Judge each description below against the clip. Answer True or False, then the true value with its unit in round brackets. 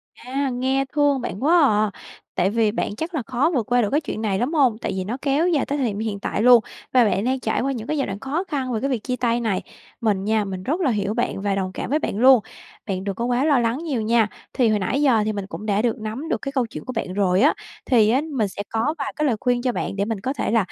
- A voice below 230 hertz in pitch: False (240 Hz)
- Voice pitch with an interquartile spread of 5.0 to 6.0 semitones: False (4.3 semitones)